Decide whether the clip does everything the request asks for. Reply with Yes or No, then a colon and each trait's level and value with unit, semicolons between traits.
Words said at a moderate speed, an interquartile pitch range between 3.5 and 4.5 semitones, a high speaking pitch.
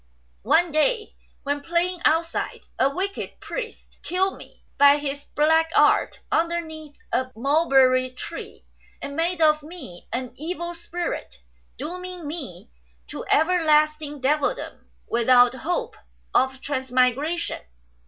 No: slow, 115 wpm; average, 4.2 semitones; very high, 305 Hz